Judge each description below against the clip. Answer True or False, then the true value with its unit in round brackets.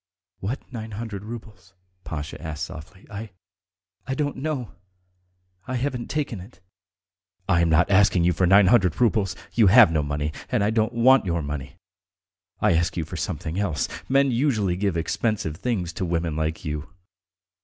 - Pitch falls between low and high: False (100 Hz)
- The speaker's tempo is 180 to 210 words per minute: False (165 wpm)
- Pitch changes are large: True (6.0 semitones)